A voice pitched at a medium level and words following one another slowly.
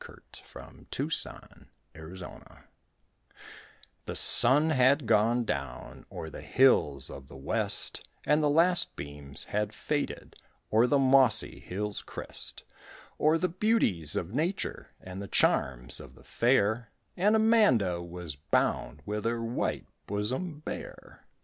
No: low, 115 Hz; slow, 130 wpm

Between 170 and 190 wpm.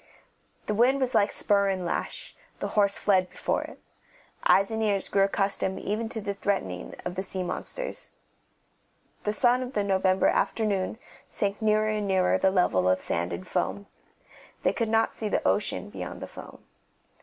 Yes: average, 175 wpm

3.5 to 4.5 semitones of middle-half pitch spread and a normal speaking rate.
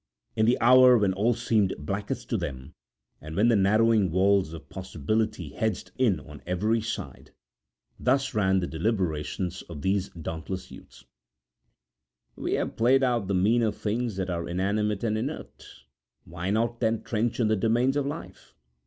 Yes: average, 3.9 semitones; average, 160 wpm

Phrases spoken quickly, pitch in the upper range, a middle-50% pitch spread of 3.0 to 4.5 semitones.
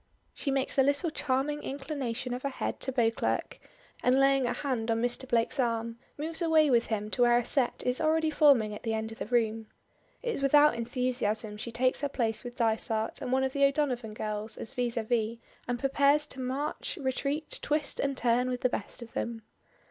Yes: fast, 210 wpm; very high, 250 Hz; average, 3.4 semitones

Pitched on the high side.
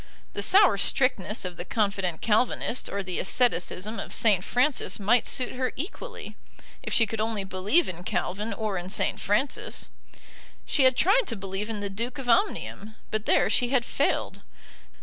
Yes: high, 215 Hz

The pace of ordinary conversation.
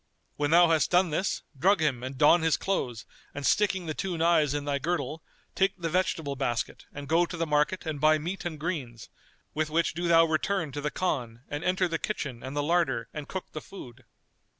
No: fast, 215 wpm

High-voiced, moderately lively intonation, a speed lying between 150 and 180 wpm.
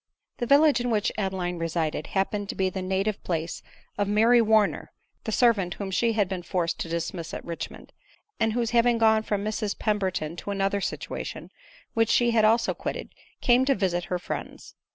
No: high, 205 Hz; average, 3.7 semitones; average, 190 wpm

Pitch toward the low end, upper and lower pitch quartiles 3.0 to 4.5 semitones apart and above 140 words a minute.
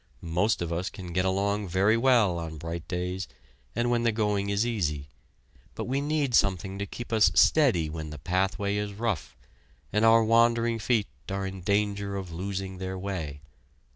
Yes: low, 100 Hz; average, 3.7 semitones; average, 175 wpm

